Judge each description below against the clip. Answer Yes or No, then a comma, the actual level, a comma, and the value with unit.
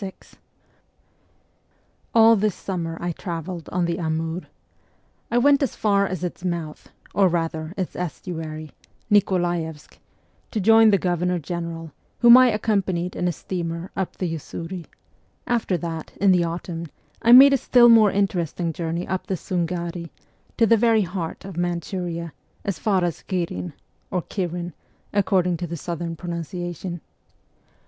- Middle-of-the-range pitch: Yes, medium, 175 Hz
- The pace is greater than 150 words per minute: No, average, 145 wpm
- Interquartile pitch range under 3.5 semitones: Yes, average, 2.8 semitones